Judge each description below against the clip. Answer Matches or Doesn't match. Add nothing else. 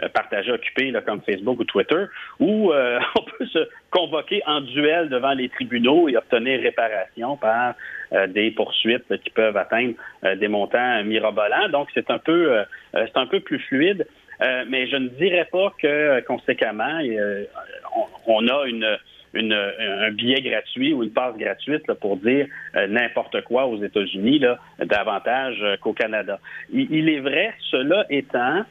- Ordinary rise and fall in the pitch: Doesn't match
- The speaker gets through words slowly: Doesn't match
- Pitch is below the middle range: Doesn't match